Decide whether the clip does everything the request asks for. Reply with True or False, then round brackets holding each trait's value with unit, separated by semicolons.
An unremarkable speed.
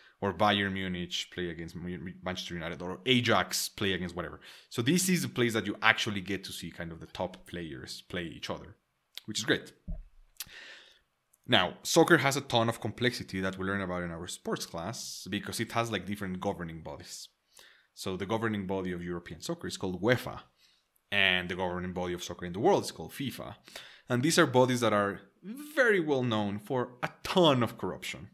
True (195 wpm)